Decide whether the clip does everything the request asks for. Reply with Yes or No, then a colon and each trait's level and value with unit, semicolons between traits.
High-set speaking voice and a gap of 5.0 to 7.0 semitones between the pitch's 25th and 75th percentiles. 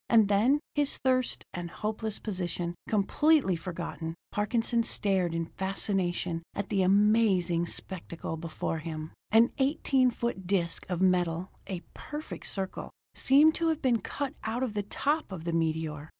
Yes: high, 195 Hz; wide, 5.5 semitones